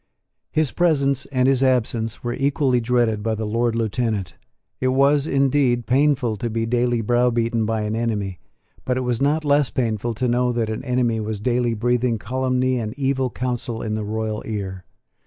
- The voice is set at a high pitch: No, low, 120 Hz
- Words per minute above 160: Yes, average, 175 wpm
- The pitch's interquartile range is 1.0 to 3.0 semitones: Yes, narrow, 2.6 semitones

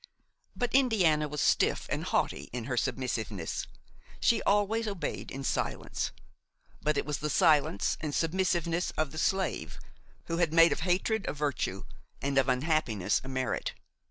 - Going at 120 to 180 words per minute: Yes, average, 155 wpm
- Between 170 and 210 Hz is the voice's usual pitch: No, medium, 155 Hz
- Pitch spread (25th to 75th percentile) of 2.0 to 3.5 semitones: No, average, 5.2 semitones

